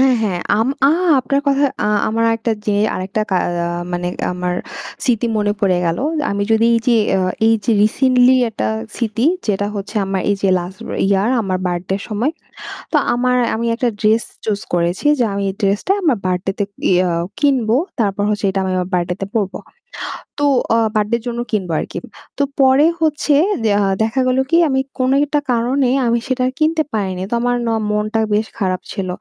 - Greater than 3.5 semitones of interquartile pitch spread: Yes, average, 4.4 semitones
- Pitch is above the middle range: Yes, high, 215 Hz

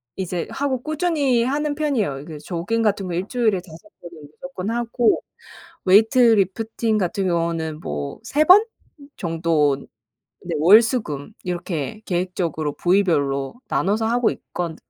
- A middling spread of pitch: No, wide, 5.8 semitones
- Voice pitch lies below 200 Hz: Yes, high, 190 Hz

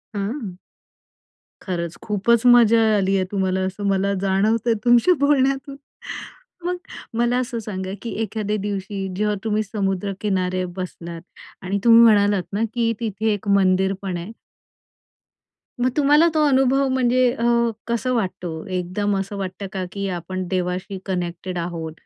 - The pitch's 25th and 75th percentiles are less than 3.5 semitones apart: No, average, 3.8 semitones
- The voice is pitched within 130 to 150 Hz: No, high, 200 Hz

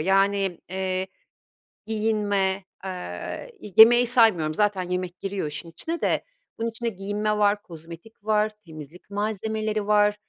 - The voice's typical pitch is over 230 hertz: No, high, 200 Hz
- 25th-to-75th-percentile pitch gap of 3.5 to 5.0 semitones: No, average, 2.8 semitones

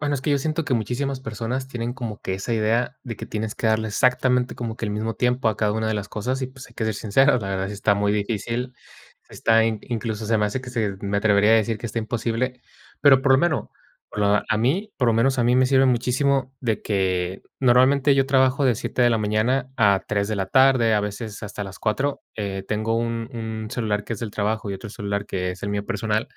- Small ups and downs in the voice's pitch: No, average, 3.5 semitones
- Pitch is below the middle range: Yes, low, 115 Hz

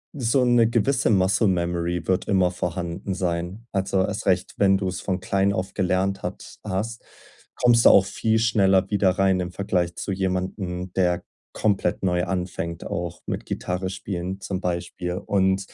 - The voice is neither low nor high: No, very low, 95 Hz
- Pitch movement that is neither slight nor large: No, narrow, 1.9 semitones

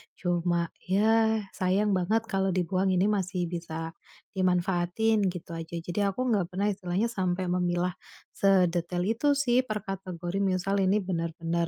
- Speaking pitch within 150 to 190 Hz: Yes, medium, 185 Hz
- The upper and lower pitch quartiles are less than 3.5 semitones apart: Yes, narrow, 2.6 semitones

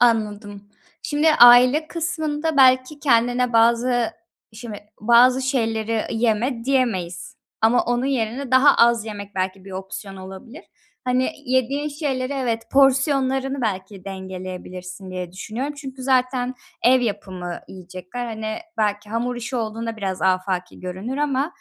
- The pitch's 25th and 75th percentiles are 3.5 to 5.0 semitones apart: Yes, average, 4.4 semitones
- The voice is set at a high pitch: Yes, high, 235 Hz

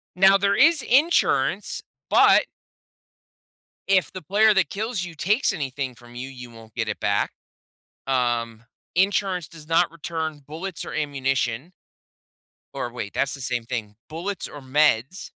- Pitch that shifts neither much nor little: No, wide, 7.3 semitones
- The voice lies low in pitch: No, medium, 150 Hz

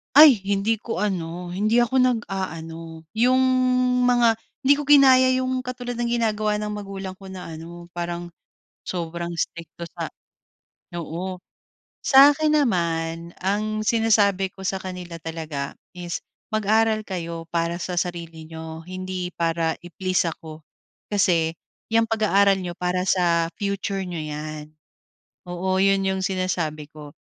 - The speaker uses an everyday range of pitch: Yes, average, 4.2 semitones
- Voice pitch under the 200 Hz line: Yes, medium, 185 Hz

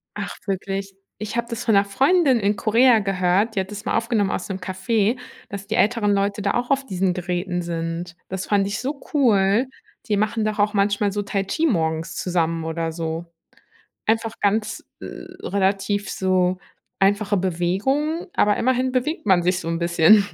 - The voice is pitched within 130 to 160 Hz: No, high, 200 Hz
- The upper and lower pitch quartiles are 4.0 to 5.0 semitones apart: No, average, 3.4 semitones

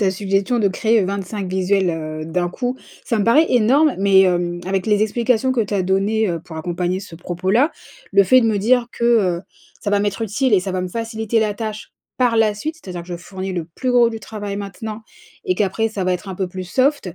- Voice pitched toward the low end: No, high, 200 Hz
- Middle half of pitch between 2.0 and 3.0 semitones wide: No, average, 3.5 semitones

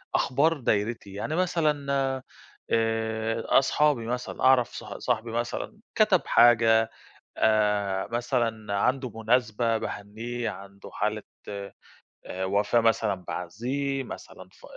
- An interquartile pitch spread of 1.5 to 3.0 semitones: No, average, 4.1 semitones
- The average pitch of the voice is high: No, low, 115 Hz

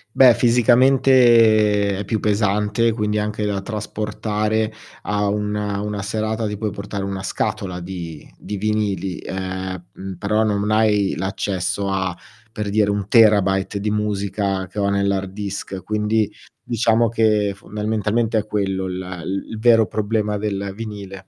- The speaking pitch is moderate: No, low, 105 Hz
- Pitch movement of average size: No, narrow, 1.8 semitones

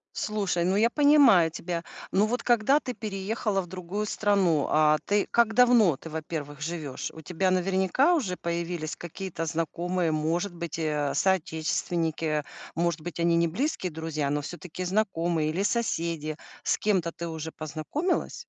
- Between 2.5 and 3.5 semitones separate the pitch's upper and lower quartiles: No, average, 4.1 semitones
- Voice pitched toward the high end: No, medium, 175 Hz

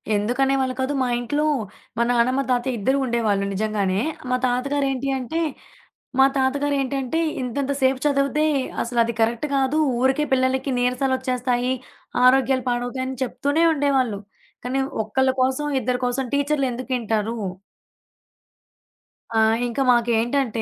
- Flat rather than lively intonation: Yes, narrow, 2.2 semitones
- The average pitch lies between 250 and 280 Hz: Yes, very high, 260 Hz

